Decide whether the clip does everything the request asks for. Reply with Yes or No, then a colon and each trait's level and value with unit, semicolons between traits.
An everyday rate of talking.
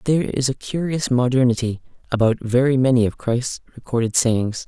Yes: average, 155 wpm